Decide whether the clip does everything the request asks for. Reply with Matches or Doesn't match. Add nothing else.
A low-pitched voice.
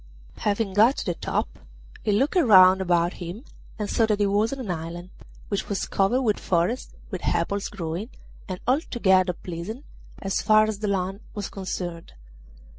Doesn't match